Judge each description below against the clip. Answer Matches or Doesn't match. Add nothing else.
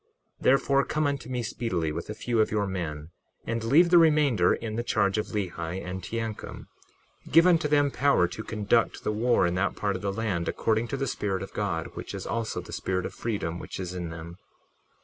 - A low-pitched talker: Matches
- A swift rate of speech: Matches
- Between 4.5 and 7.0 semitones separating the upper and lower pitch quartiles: Matches